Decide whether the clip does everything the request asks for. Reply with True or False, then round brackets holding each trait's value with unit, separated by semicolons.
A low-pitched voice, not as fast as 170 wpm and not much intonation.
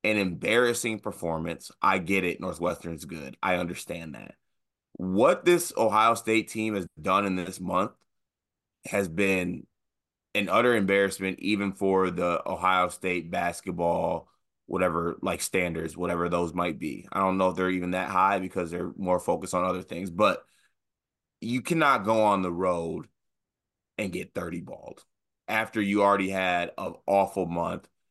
True (95 Hz; 155 wpm; 2.3 semitones)